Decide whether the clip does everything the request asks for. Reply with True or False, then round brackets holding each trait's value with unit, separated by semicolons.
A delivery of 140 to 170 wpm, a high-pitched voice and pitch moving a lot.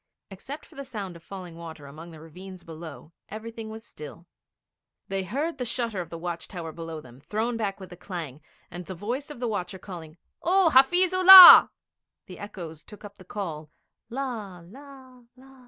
False (185 wpm; 195 Hz; 6.9 semitones)